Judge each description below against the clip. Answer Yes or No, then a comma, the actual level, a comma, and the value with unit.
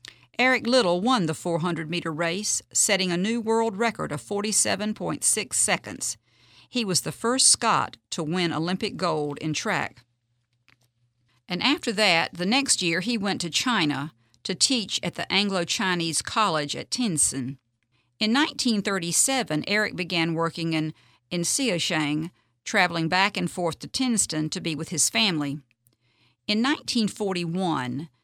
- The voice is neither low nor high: Yes, medium, 175 Hz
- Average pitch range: No, wide, 5.8 semitones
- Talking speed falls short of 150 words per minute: Yes, average, 140 wpm